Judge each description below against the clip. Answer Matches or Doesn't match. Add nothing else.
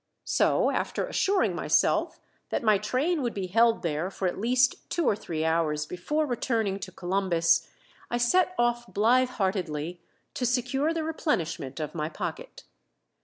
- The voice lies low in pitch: Doesn't match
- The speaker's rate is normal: Matches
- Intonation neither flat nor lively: Doesn't match